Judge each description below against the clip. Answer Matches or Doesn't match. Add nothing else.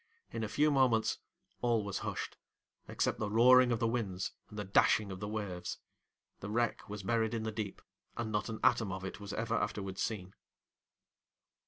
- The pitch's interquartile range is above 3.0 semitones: Doesn't match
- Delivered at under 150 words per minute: Doesn't match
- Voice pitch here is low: Matches